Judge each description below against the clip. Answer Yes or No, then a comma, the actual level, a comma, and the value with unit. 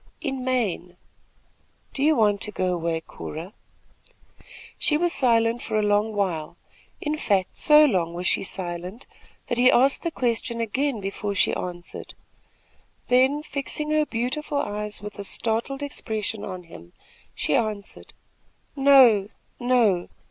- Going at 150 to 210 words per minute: No, average, 140 wpm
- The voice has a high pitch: Yes, high, 220 Hz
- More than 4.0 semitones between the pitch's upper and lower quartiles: Yes, wide, 5.6 semitones